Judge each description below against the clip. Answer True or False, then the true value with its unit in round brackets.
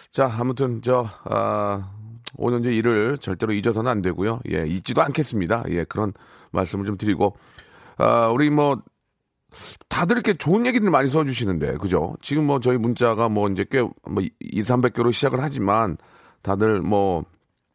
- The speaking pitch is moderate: False (115 Hz)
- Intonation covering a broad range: False (4.8 semitones)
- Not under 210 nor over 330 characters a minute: True (300 characters per minute)